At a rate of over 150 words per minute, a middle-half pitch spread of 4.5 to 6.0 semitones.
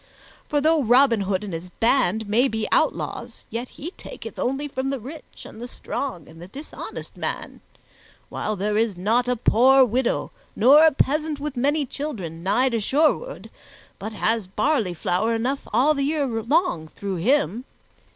Yes: average, 170 wpm; average, 5.1 semitones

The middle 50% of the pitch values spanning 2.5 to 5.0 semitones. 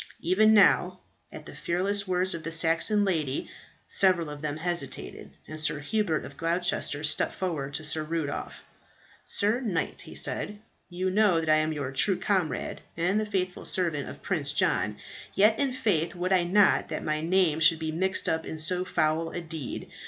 Yes: average, 3.4 semitones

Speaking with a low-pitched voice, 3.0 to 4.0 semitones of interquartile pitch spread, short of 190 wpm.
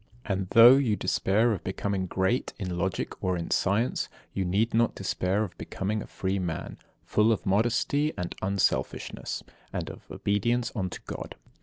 Yes: low, 100 Hz; average, 3.3 semitones; average, 160 wpm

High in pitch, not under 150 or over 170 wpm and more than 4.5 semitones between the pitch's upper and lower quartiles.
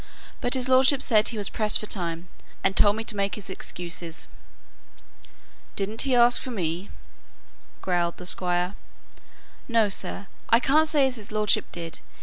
Yes: high, 210 Hz; average, 160 wpm; average, 5.2 semitones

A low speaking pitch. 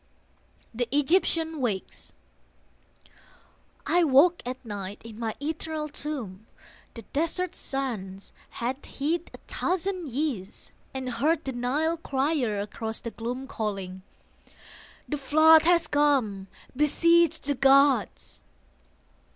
No: very high, 275 Hz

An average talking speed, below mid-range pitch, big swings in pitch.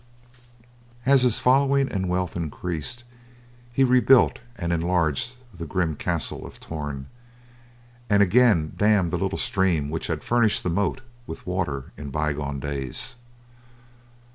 No: slow, 130 wpm; very low, 90 Hz; wide, 7.6 semitones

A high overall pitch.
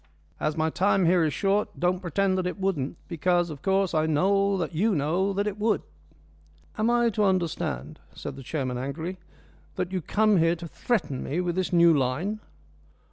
No: medium, 180 Hz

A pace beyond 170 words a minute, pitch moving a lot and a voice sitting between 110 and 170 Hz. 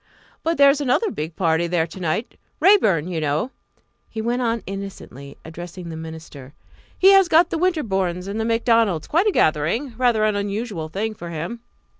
No: average, 180 wpm; wide, 6.9 semitones; high, 200 Hz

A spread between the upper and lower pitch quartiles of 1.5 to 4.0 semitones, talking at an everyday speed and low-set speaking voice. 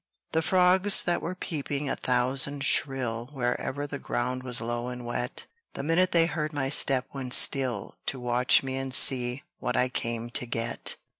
Yes: average, 2.8 semitones; average, 175 wpm; low, 130 Hz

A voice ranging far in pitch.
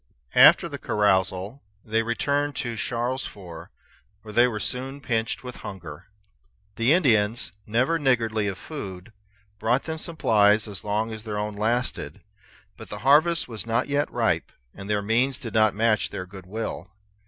No: average, 3.7 semitones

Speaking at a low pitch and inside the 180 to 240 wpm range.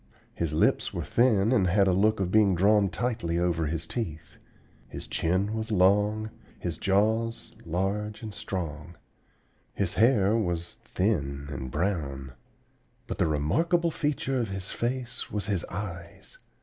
No: low, 100 Hz; average, 145 wpm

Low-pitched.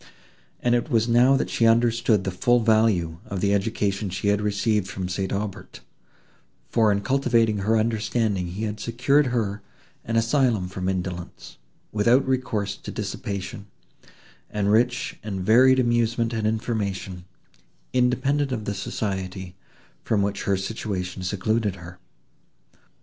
Yes: low, 105 Hz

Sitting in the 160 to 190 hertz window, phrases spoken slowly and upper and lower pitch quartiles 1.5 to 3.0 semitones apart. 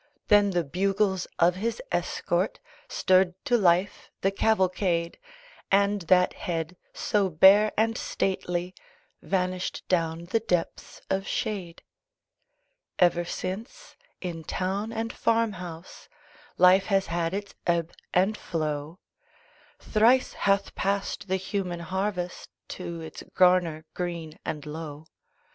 Yes: medium, 185 Hz; slow, 115 wpm; average, 2.7 semitones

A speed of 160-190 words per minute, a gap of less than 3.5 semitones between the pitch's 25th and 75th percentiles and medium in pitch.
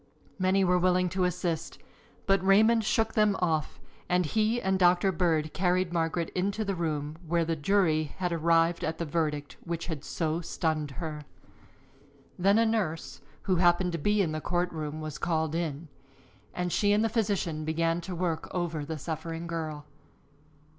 Yes: average, 170 wpm; average, 2.9 semitones; medium, 170 Hz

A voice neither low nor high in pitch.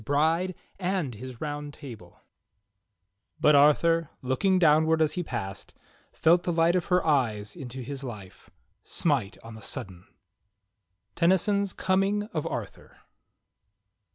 Yes: medium, 150 Hz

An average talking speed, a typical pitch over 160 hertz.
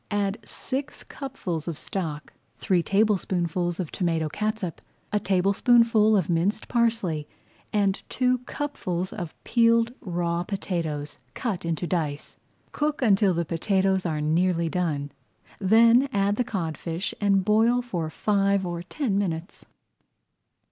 No: slow, 125 wpm; high, 190 Hz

